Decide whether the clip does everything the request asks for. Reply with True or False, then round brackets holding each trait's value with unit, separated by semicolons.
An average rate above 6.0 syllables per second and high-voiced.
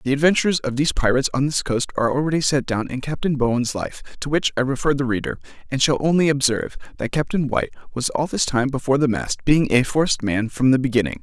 False (6.5 syllables/s; 135 Hz)